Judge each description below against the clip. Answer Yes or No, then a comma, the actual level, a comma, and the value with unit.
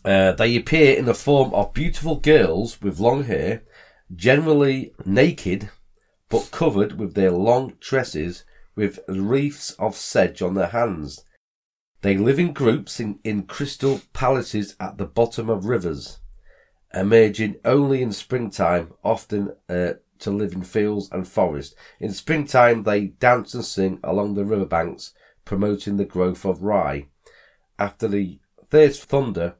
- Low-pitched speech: Yes, low, 105 Hz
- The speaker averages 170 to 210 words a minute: No, average, 145 wpm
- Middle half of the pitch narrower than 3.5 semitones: No, average, 4.9 semitones